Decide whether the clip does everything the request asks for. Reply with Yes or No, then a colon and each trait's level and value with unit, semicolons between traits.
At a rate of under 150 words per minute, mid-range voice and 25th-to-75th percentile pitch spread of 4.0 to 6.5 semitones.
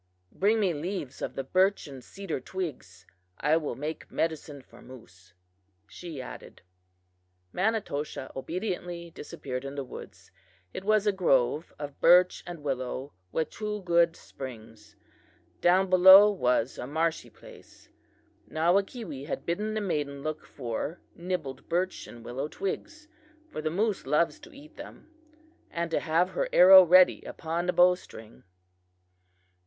Yes: average, 140 wpm; medium, 165 Hz; wide, 5.4 semitones